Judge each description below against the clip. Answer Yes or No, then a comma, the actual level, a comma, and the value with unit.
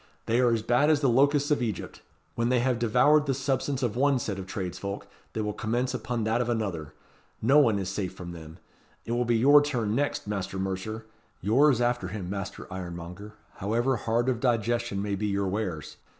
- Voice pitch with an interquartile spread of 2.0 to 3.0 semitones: No, average, 4.2 semitones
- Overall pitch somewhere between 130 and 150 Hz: No, low, 115 Hz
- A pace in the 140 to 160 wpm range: No, average, 200 wpm